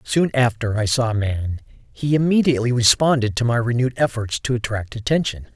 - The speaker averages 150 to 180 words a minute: Yes, average, 175 wpm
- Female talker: No, male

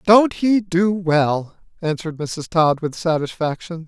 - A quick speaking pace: No, average, 140 wpm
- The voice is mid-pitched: Yes, medium, 170 Hz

